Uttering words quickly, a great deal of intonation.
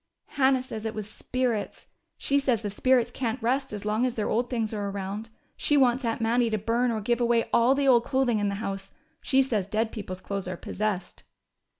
No: fast, 215 wpm; average, 3.2 semitones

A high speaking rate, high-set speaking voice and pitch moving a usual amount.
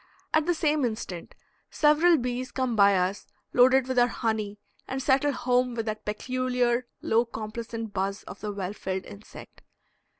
No: average, 160 wpm; high, 240 Hz; average, 3.5 semitones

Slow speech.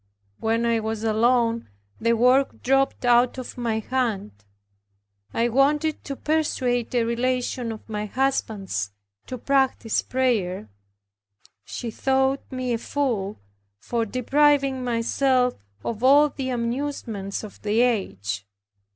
Yes: slow, 120 wpm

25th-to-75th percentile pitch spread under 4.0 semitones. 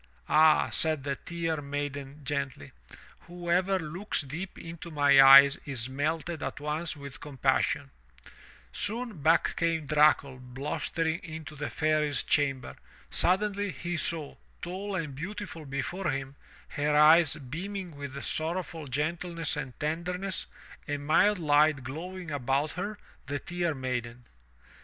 Yes: average, 3.5 semitones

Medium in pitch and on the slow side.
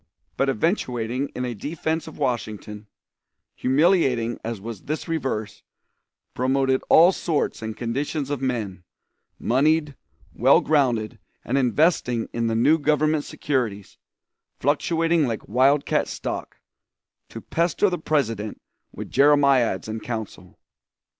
No: low, 130 Hz; slow, 120 wpm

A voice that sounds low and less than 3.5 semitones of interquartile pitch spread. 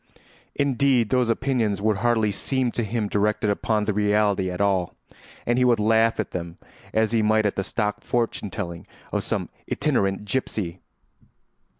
Yes: low, 105 Hz; average, 2.8 semitones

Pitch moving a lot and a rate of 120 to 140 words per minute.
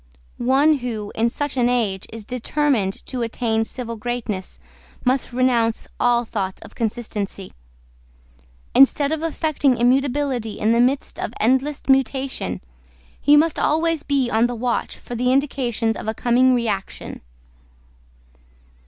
No: average, 3.3 semitones; slow, 135 wpm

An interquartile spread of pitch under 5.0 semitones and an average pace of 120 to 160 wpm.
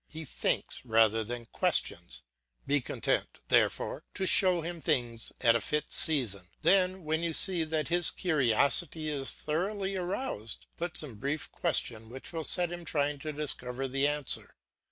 No: wide, 5.6 semitones; average, 155 wpm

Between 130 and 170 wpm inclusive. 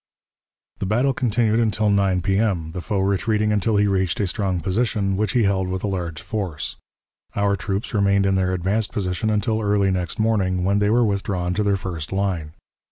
No: average, 190 wpm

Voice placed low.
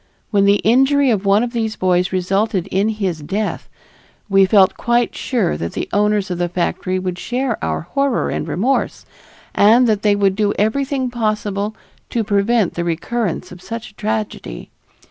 No: high, 210 Hz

